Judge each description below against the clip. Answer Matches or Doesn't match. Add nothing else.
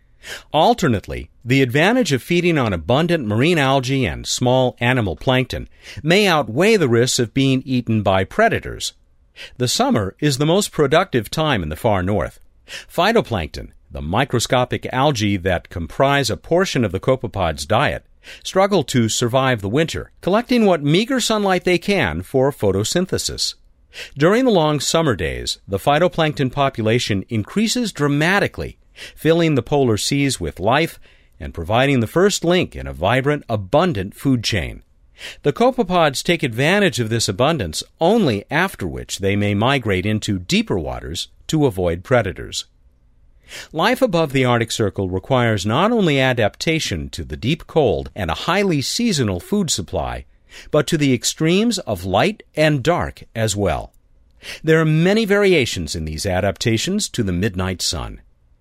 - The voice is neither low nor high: Doesn't match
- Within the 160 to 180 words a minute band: Doesn't match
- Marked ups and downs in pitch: Matches